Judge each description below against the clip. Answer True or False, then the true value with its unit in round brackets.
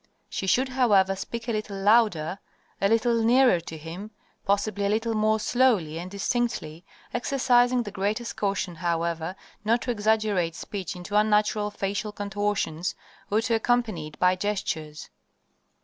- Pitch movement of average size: True (3.8 semitones)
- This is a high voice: True (205 Hz)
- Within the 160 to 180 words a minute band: False (145 wpm)